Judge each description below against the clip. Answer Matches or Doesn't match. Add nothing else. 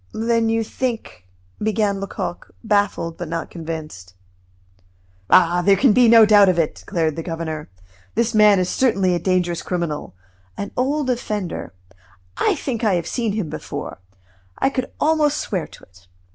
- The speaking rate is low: Doesn't match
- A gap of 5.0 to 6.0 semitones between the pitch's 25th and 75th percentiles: Matches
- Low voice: Doesn't match